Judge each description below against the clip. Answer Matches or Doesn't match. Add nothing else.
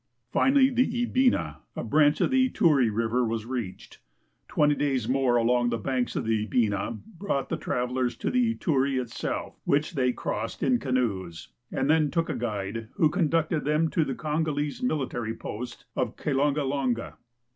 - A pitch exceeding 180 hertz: Doesn't match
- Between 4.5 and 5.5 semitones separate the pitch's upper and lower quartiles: Matches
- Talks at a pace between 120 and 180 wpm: Matches